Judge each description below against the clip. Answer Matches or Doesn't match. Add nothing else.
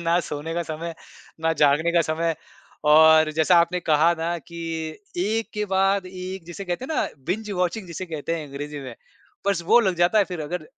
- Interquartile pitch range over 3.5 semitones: Doesn't match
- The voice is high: Doesn't match